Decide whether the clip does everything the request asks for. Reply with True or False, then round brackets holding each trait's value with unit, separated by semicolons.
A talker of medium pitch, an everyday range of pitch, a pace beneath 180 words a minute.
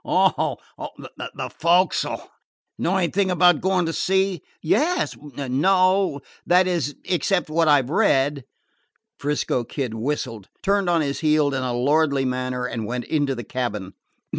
False (150 Hz; 5.8 semitones; 140 wpm)